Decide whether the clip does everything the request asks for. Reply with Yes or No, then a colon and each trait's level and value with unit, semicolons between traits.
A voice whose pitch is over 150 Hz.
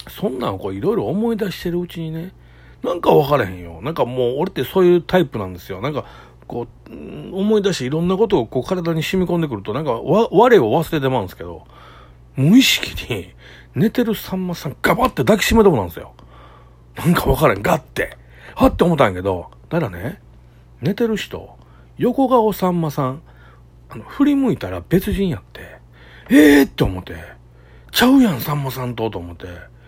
No: medium, 140 Hz